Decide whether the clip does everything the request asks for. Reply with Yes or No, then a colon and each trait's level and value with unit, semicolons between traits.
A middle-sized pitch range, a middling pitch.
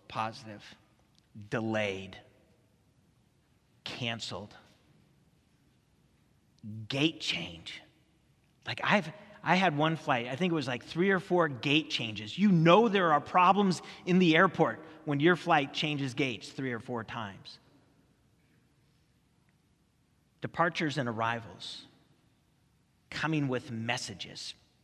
No: wide, 6.5 semitones; medium, 145 Hz